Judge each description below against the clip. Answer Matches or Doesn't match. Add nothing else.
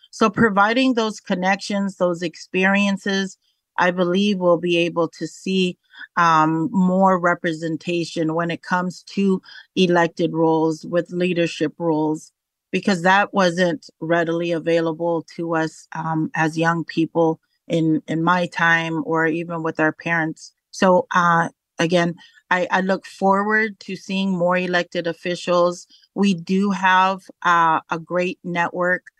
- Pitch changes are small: Matches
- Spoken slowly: Matches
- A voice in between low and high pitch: Matches